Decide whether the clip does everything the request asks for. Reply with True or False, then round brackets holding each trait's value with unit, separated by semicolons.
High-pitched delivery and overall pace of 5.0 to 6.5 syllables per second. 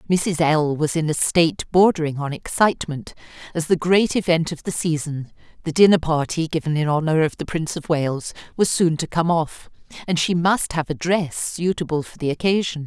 False (165 Hz; 5.3 syllables/s)